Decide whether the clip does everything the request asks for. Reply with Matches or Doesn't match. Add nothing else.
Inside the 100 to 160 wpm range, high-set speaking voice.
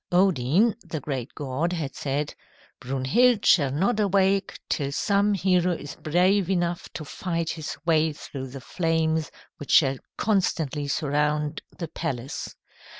Doesn't match